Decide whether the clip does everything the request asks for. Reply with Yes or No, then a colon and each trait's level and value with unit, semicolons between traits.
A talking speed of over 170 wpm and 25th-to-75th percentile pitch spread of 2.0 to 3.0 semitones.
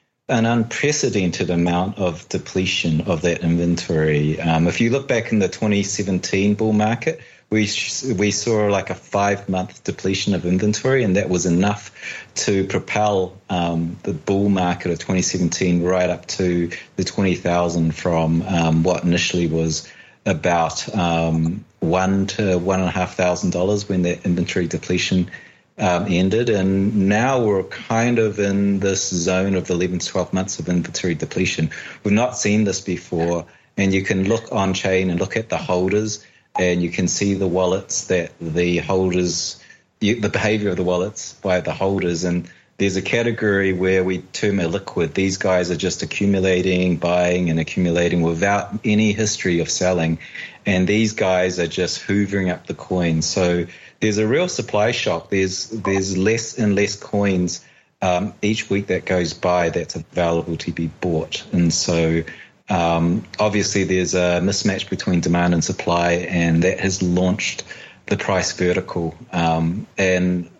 No: average, 165 wpm; narrow, 2.5 semitones